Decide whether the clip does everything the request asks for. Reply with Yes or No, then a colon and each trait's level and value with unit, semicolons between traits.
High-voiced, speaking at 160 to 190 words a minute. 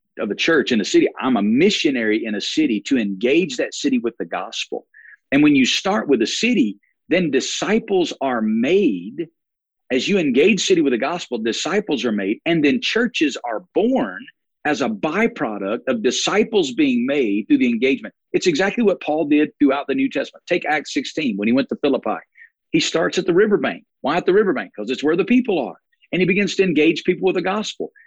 No: high, 220 Hz; fast, 205 wpm